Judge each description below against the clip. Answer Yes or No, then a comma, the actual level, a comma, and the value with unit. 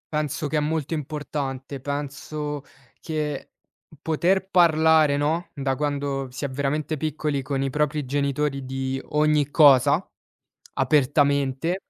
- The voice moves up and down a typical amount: No, narrow, 1.9 semitones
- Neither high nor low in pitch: Yes, medium, 145 Hz